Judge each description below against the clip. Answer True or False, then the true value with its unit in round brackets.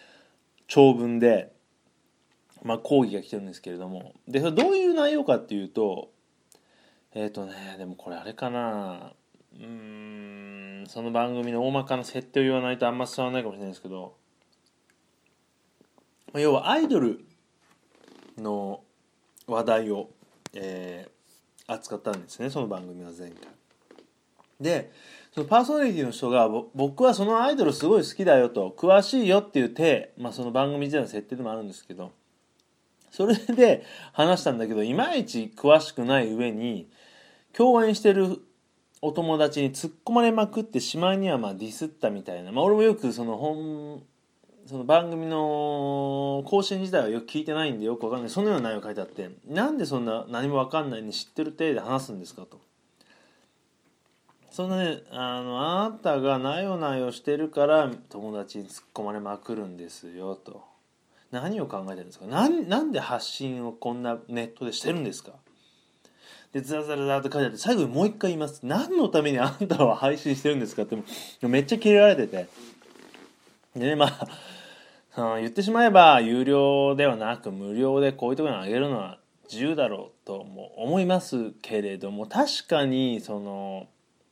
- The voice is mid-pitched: False (130 Hz)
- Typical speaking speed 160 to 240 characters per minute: False (335 characters per minute)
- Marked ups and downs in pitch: True (6.0 semitones)